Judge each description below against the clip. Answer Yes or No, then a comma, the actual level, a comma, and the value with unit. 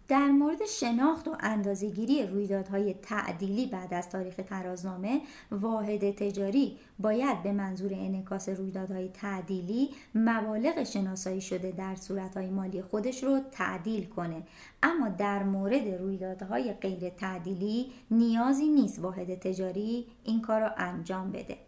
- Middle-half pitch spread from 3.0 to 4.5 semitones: Yes, average, 3.7 semitones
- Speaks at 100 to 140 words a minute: Yes, average, 120 wpm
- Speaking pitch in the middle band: No, high, 200 Hz